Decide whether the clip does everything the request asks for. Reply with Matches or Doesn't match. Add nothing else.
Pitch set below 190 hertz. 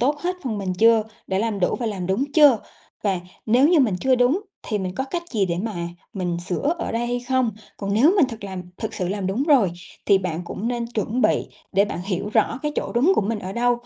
Doesn't match